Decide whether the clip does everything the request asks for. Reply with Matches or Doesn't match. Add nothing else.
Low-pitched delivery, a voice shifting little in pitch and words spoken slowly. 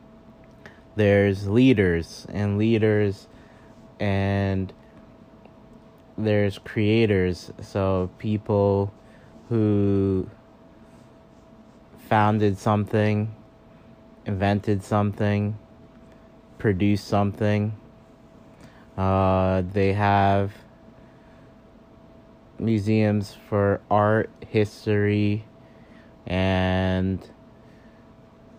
Matches